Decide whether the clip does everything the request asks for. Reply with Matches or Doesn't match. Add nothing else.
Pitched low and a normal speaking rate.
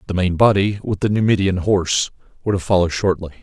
Matches